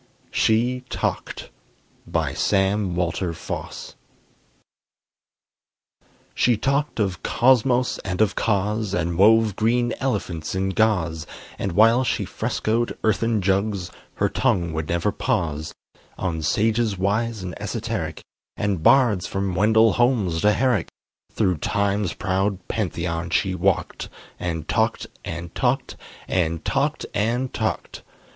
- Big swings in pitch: No, average, 4.1 semitones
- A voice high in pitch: No, low, 100 Hz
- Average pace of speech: No, slow, 120 wpm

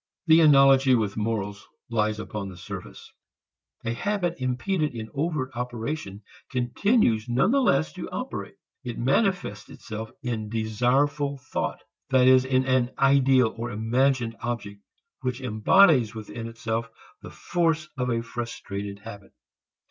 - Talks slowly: Yes, slow, 125 wpm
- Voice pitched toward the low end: Yes, low, 120 Hz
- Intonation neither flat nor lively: Yes, average, 3.7 semitones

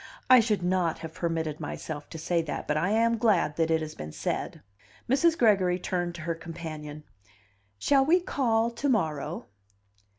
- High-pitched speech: No, medium, 175 Hz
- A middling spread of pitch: No, wide, 6.1 semitones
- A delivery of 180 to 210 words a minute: No, average, 170 wpm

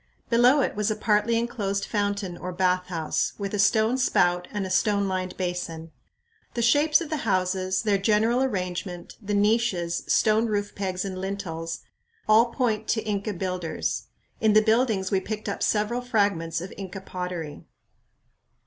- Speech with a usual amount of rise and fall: Yes, average, 3.2 semitones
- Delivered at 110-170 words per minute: Yes, average, 160 wpm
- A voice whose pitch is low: No, high, 200 Hz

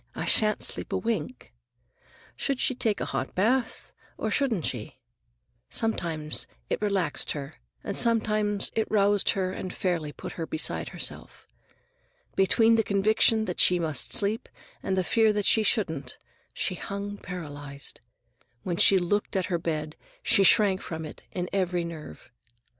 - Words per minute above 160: No, average, 155 wpm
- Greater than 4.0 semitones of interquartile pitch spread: Yes, average, 4.6 semitones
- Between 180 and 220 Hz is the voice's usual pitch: Yes, high, 190 Hz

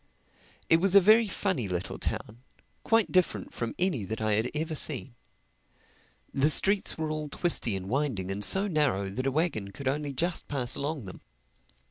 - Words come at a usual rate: Yes, average, 175 wpm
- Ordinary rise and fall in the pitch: No, wide, 7.6 semitones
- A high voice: No, medium, 145 Hz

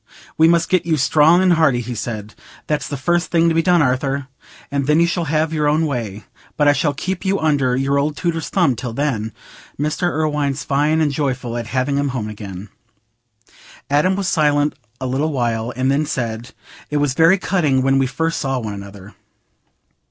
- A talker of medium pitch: Yes, medium, 145 Hz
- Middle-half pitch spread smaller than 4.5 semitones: Yes, average, 3.9 semitones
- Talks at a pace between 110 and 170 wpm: No, average, 195 wpm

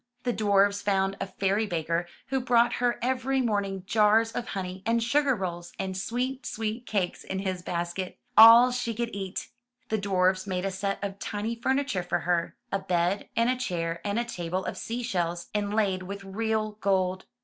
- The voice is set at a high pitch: Yes, high, 200 Hz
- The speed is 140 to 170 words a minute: No, average, 185 wpm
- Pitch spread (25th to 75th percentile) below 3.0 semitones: No, average, 3.7 semitones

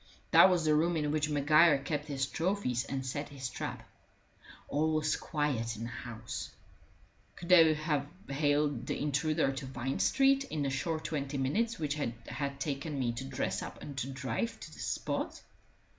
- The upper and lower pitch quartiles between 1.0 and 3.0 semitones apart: Yes, average, 2.7 semitones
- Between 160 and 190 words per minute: Yes, average, 175 wpm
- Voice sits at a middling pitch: Yes, medium, 145 Hz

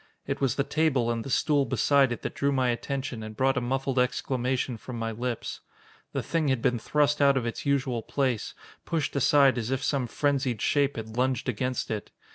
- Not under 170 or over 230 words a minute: Yes, fast, 205 wpm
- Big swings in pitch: No, narrow, 2.6 semitones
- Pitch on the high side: No, low, 130 Hz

